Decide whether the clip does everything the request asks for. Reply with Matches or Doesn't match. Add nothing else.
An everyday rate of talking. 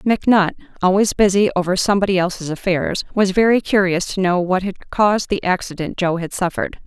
Matches